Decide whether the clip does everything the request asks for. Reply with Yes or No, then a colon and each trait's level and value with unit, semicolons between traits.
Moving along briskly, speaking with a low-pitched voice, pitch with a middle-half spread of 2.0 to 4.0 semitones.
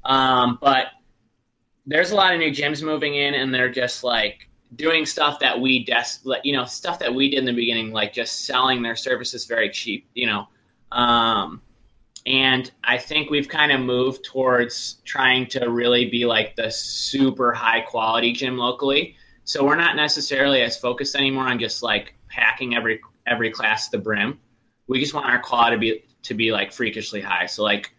No: average, 190 wpm; low, 125 Hz; narrow, 2.6 semitones